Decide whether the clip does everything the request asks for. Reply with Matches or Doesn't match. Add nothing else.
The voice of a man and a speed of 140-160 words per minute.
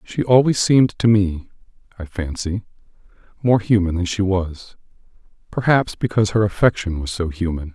Matches